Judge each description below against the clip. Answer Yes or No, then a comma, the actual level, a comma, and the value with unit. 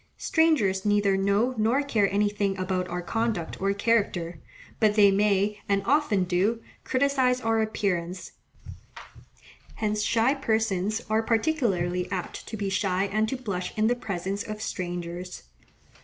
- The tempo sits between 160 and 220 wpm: No, average, 140 wpm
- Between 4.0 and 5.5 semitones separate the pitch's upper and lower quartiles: No, average, 3.1 semitones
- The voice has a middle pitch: No, high, 205 Hz